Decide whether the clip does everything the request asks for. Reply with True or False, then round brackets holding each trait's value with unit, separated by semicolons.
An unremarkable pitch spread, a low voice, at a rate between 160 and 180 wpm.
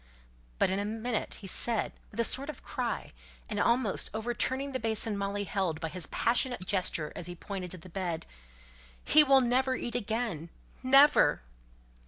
False (5.0 semitones; 220 Hz; 170 wpm)